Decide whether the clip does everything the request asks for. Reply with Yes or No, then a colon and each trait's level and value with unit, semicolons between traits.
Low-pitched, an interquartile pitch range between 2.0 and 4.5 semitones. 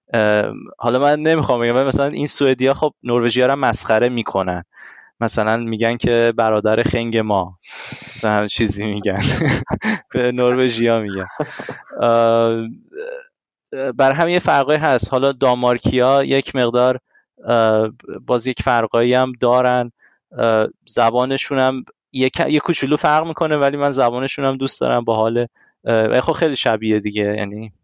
Yes: low, 125 Hz; average, 3.2 semitones